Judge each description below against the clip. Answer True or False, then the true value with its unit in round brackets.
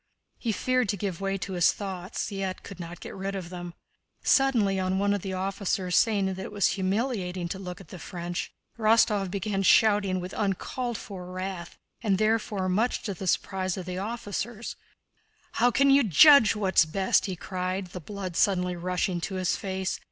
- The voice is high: True (195 Hz)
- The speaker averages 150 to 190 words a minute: True (185 wpm)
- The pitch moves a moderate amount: False (2.2 semitones)